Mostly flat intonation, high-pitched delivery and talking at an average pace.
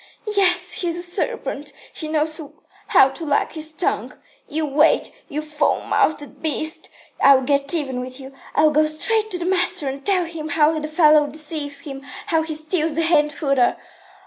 Yes: narrow, 2.3 semitones; very high, 310 Hz; average, 180 wpm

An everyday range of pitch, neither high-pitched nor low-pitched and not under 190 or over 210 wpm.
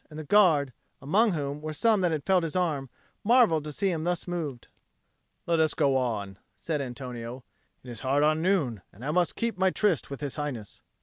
Yes: average, 4.8 semitones; medium, 155 Hz; fast, 205 wpm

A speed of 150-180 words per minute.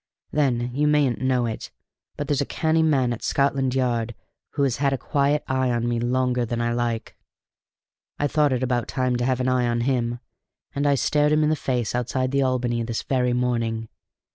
No: fast, 205 wpm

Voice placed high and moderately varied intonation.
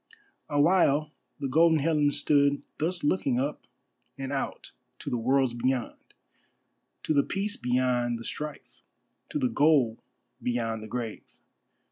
No: medium, 140 Hz; average, 3.7 semitones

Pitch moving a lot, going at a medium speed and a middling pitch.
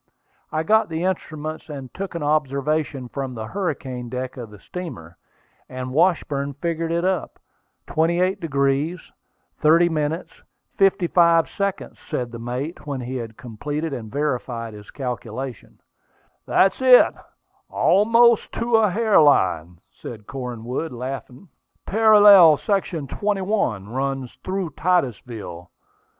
No: wide, 6.2 semitones; slow, 115 wpm; medium, 150 Hz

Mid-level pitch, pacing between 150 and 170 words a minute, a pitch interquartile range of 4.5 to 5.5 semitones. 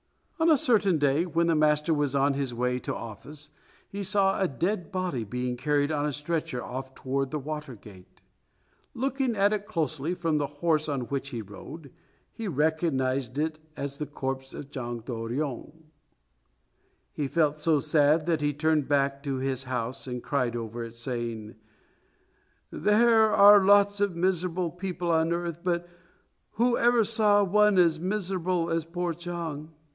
Yes: medium, 155 Hz; average, 165 wpm; average, 5.0 semitones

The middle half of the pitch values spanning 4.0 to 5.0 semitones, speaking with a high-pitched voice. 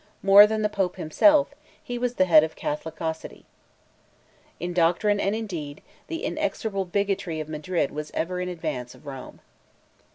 No: average, 4.7 semitones; medium, 180 Hz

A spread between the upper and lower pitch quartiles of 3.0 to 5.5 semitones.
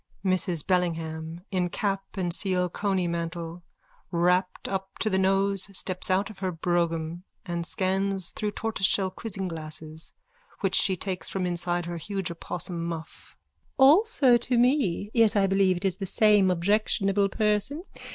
No: narrow, 2.5 semitones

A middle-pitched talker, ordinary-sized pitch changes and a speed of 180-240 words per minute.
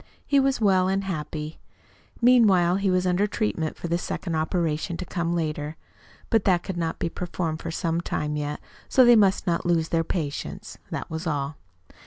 Yes: medium, 175 Hz; average, 3.3 semitones; average, 185 wpm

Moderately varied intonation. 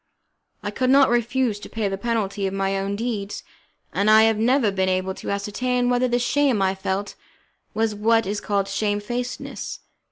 Yes: average, 3.5 semitones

